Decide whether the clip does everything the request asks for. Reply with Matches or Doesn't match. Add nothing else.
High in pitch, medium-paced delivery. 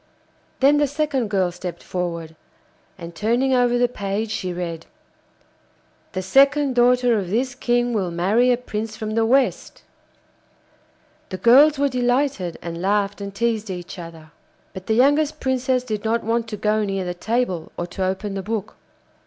Matches